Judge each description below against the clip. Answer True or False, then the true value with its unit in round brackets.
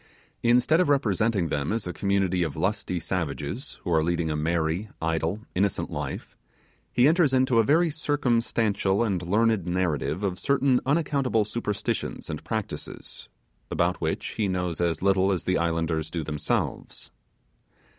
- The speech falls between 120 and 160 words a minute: True (145 wpm)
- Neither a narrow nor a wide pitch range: False (5.9 semitones)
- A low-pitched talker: True (95 Hz)